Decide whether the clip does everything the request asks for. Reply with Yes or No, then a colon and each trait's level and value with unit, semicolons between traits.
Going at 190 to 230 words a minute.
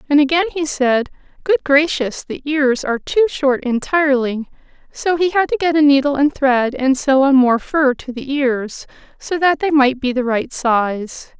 Yes: average, 195 wpm